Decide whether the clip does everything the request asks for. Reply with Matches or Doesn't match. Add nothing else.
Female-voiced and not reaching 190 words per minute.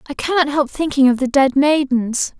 Doesn't match